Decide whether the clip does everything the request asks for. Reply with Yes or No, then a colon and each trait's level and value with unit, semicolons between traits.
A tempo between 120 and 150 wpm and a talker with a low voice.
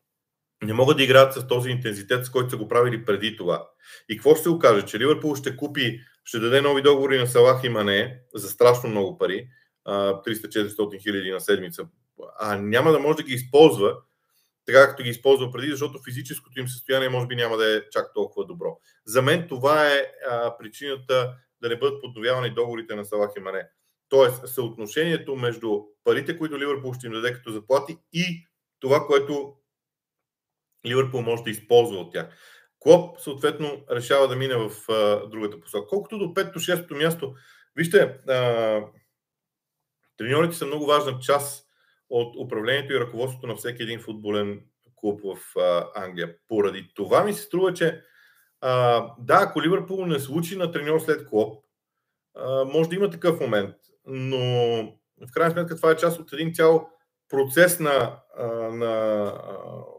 No: fast, 165 wpm; low, 130 Hz